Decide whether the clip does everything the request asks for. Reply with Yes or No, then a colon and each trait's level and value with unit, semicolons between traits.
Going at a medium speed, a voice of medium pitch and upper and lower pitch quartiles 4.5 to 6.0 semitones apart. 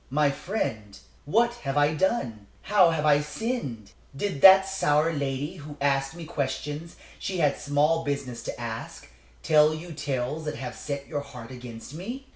No: average, 165 wpm; medium, 145 Hz; average, 3.3 semitones